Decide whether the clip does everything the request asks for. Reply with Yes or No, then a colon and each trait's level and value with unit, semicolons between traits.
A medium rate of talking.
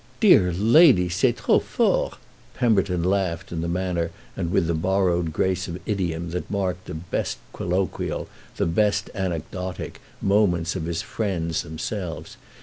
Yes: average, 145 wpm